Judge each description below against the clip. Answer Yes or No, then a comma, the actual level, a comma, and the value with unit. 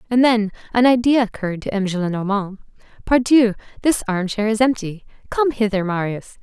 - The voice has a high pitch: Yes, high, 215 Hz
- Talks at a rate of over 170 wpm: No, average, 140 wpm